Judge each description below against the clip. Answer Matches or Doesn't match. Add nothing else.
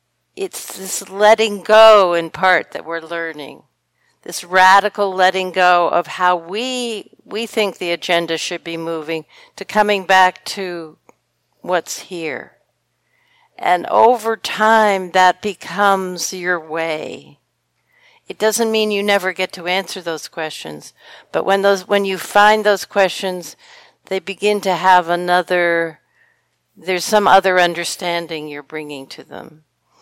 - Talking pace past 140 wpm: Doesn't match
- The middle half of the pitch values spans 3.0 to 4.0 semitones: Matches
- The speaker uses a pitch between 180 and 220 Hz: Matches